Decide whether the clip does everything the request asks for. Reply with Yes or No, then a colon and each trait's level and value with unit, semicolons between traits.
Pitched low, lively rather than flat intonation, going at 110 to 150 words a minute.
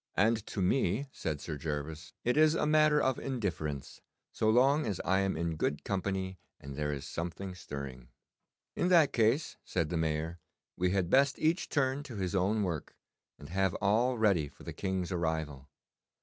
No: very low, 95 Hz; wide, 7.3 semitones; average, 175 wpm